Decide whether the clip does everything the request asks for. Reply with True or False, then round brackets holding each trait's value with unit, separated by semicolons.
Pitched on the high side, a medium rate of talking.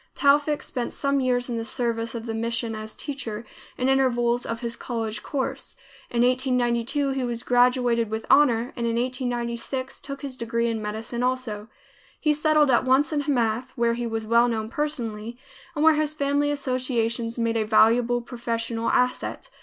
True (240 Hz; 170 wpm)